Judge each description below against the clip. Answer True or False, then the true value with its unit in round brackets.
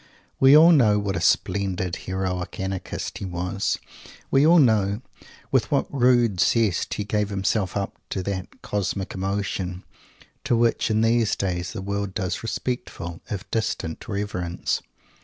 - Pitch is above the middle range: False (100 Hz)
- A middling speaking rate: True (145 wpm)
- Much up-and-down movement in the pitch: False (3.3 semitones)